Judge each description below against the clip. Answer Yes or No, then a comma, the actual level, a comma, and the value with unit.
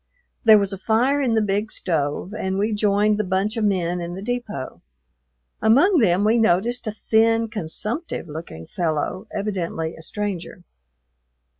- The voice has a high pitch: Yes, high, 205 Hz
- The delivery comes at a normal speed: Yes, average, 155 wpm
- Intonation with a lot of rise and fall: No, average, 3.9 semitones